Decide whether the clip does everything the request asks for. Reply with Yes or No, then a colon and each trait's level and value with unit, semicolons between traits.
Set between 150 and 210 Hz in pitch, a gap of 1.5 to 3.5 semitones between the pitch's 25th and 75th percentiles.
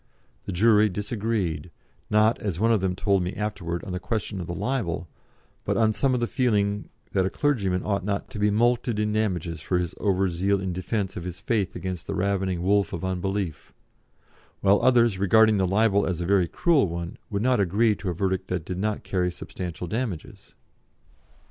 No: low, 100 Hz; average, 2.9 semitones